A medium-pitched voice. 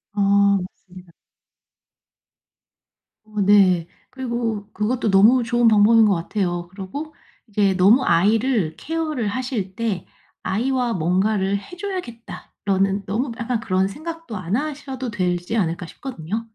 No: high, 210 Hz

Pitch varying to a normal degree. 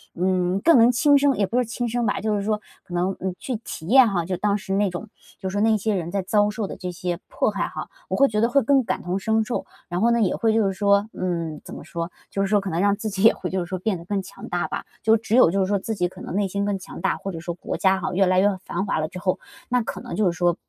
Yes: average, 3.3 semitones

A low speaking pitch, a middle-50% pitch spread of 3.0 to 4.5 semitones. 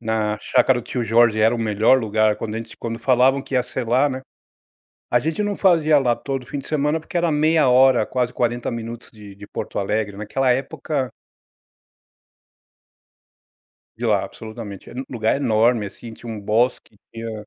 Yes: low, 120 Hz; average, 3.3 semitones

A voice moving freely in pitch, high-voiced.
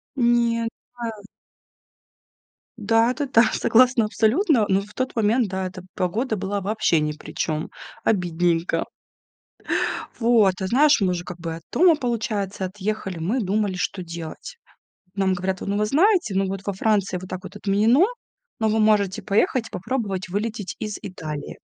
No: average, 3.7 semitones; high, 205 Hz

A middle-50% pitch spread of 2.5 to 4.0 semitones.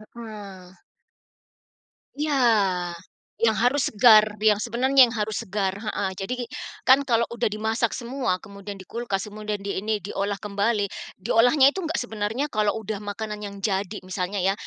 Yes: average, 3.0 semitones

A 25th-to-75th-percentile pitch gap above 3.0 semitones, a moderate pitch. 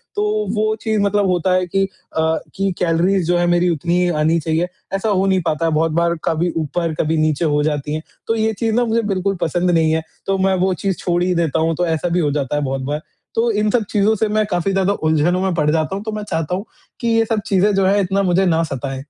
Yes: average, 3.7 semitones; medium, 180 Hz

